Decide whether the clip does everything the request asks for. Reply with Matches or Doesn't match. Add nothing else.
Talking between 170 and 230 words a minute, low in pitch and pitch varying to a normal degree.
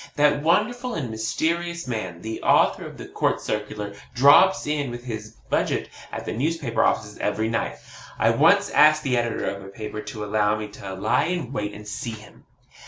Doesn't match